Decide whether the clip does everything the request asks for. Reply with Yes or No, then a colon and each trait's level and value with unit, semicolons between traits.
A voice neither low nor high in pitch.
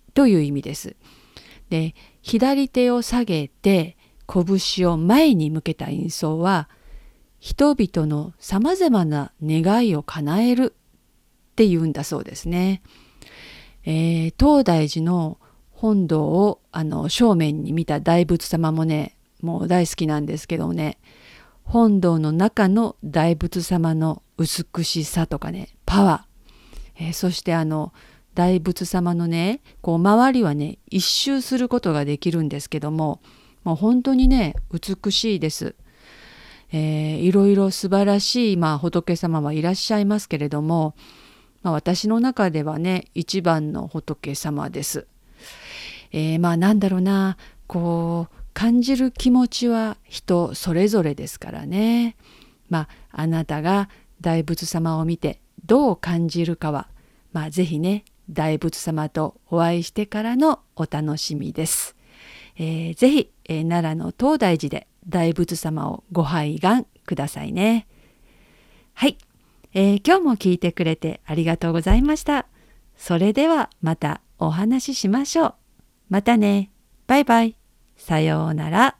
Yes: medium, 175 Hz